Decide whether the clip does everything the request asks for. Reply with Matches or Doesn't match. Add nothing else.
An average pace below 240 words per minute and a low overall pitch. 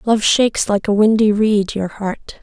Doesn't match